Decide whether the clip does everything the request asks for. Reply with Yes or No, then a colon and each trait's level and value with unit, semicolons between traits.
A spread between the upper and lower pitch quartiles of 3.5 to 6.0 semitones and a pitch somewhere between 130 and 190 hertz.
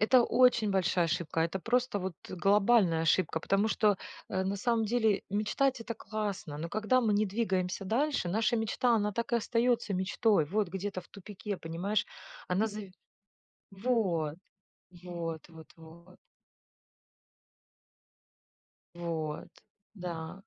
No: average, 4.1 semitones; high, 200 Hz